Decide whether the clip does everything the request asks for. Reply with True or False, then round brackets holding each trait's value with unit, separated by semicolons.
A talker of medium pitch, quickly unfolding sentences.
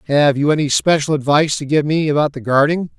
True (145 Hz; 220 wpm)